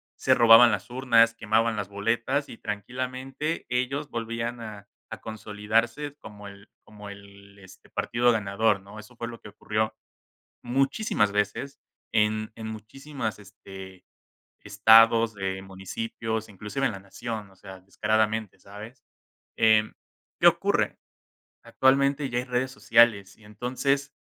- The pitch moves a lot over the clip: No, average, 3.0 semitones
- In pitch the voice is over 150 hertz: No, low, 110 Hz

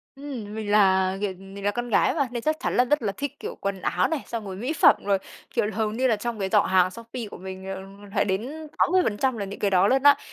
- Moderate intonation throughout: Yes, average, 4.7 semitones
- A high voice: Yes, high, 210 Hz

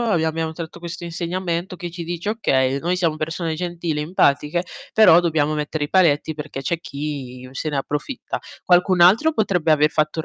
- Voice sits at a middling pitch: Yes, medium, 165 Hz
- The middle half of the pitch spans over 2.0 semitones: Yes, average, 2.7 semitones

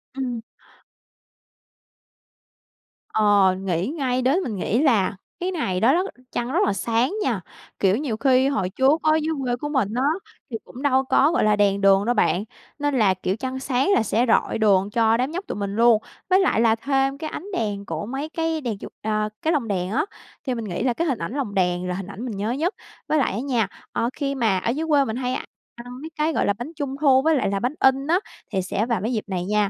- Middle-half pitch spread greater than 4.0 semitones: Yes, average, 5.3 semitones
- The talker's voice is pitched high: Yes, high, 240 Hz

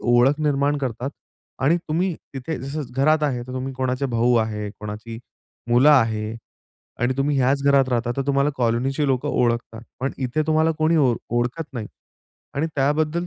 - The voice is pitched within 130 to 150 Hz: Yes, low, 135 Hz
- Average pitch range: Yes, average, 3.4 semitones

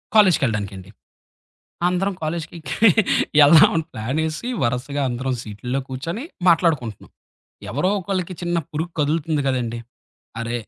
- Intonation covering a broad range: Yes, wide, 5.8 semitones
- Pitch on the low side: No, medium, 150 Hz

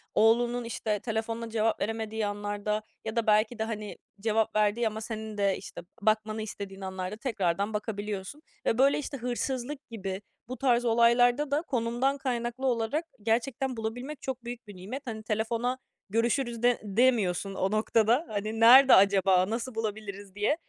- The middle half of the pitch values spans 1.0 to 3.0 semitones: Yes, narrow, 2.6 semitones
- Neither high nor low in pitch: No, high, 225 Hz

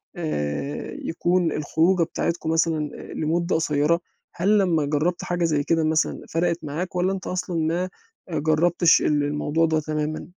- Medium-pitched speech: Yes, medium, 165 Hz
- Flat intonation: Yes, narrow, 2.3 semitones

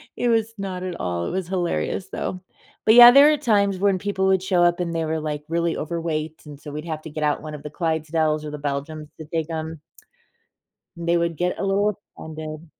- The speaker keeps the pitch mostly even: No, average, 3.6 semitones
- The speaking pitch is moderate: Yes, medium, 165 Hz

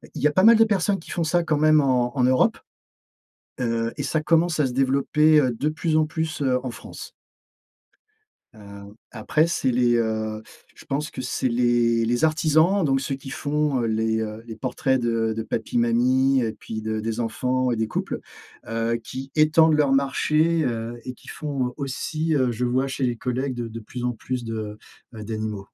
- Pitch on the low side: Yes, low, 130 Hz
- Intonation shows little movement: No, average, 4.7 semitones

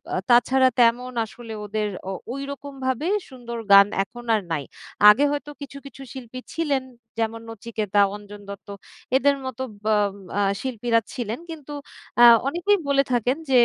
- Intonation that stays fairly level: No, average, 3.7 semitones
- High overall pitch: Yes, high, 245 Hz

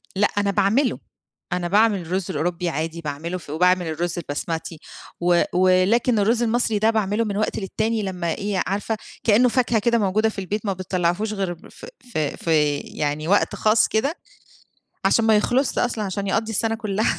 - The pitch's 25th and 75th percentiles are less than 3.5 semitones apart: No, average, 4.0 semitones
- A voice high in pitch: Yes, high, 195 Hz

